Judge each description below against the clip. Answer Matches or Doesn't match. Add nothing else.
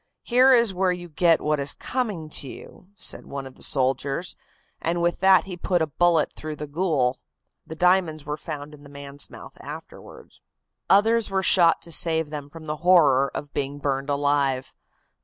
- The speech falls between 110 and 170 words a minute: Doesn't match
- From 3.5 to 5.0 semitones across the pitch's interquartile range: Matches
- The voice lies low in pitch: Doesn't match